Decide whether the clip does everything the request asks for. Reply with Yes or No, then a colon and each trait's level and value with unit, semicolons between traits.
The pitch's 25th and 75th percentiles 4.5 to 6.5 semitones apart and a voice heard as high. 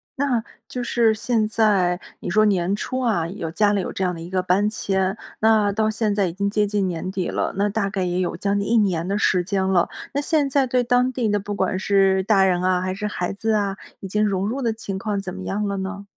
No: narrow, 2.5 semitones; high, 200 Hz